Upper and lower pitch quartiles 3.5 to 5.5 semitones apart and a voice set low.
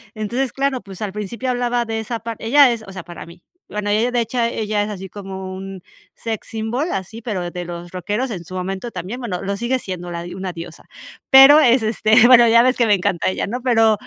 No: average, 4.1 semitones; high, 215 Hz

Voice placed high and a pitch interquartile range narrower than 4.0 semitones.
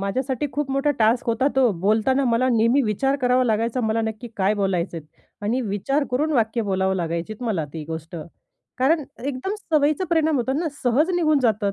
No: high, 235 Hz; average, 4.9 semitones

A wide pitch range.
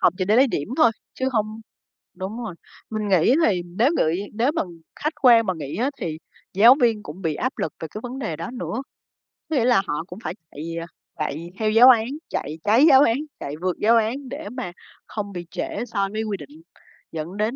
Yes: wide, 5.7 semitones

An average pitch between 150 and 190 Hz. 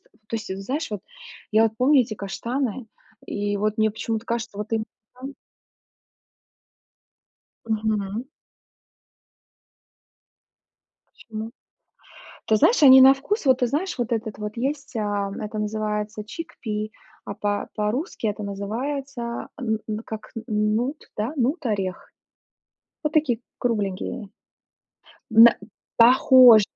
No: high, 220 Hz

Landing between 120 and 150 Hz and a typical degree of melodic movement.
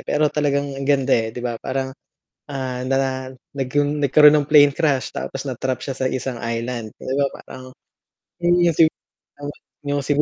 No: low, 135 Hz; narrow, 1.9 semitones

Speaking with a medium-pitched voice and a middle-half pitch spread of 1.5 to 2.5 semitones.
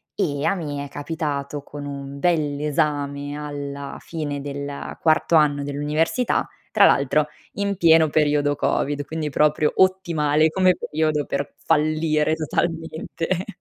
Yes: medium, 150 Hz; narrow, 2.1 semitones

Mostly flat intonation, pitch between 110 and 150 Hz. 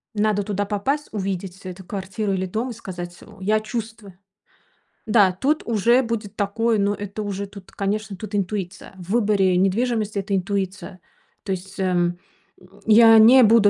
No: narrow, 2.3 semitones; high, 205 Hz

